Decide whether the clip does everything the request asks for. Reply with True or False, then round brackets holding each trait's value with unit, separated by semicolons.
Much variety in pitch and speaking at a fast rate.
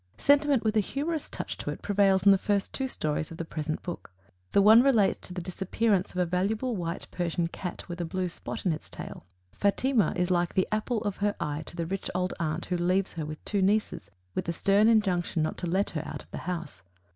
False (3.4 semitones; 235 wpm)